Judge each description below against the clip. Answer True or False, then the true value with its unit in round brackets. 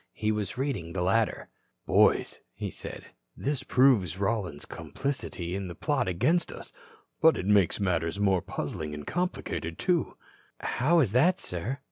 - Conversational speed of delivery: True (150 wpm)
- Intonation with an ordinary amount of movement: False (7.4 semitones)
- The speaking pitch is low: True (105 Hz)